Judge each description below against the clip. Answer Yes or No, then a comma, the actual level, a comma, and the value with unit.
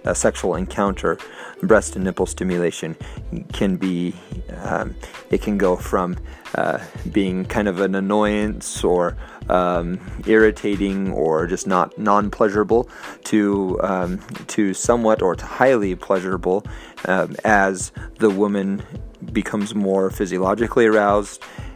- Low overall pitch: Yes, low, 100 Hz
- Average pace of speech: No, slow, 120 wpm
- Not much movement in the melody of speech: Yes, narrow, 2.1 semitones